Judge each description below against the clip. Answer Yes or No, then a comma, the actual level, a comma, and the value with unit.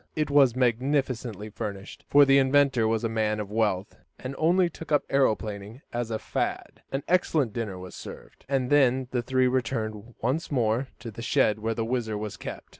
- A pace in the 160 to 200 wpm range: Yes, average, 190 wpm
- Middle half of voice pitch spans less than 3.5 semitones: No, average, 3.9 semitones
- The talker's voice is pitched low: Yes, low, 120 Hz